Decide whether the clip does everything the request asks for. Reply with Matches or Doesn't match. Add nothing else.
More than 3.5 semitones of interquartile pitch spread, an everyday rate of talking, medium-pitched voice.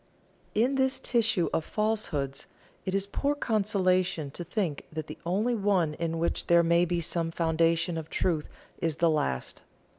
Matches